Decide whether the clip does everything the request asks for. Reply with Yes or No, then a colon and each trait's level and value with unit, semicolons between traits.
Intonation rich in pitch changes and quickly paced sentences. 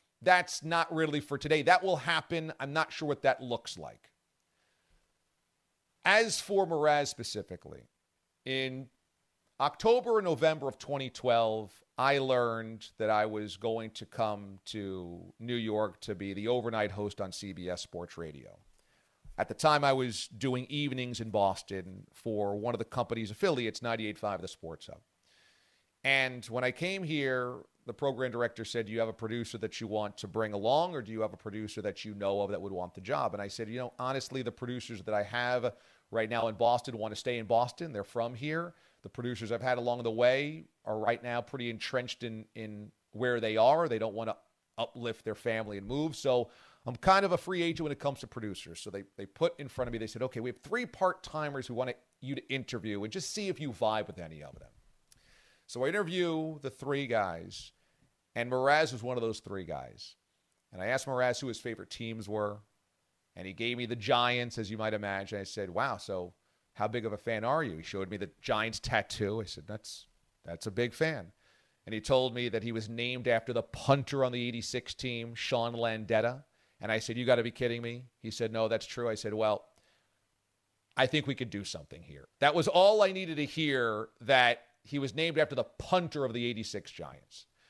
No: average, 3.7 semitones; fast, 210 wpm